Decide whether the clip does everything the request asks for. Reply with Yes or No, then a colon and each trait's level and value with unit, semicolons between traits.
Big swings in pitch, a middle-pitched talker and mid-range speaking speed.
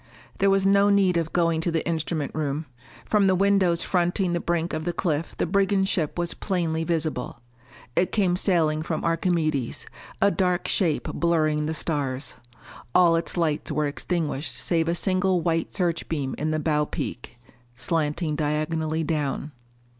No: average, 2.7 semitones; medium, 165 Hz; average, 160 wpm